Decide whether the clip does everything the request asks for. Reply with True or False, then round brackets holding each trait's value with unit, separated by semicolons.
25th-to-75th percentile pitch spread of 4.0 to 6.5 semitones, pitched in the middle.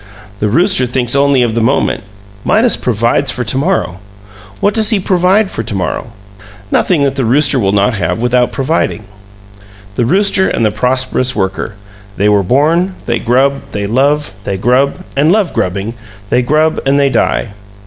False (5.2 semitones; 130 Hz)